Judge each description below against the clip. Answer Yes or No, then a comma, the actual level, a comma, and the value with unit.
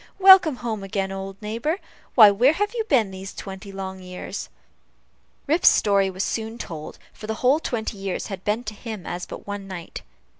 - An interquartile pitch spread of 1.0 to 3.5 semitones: No, average, 3.9 semitones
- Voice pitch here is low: No, high, 210 Hz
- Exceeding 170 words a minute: Yes, average, 185 wpm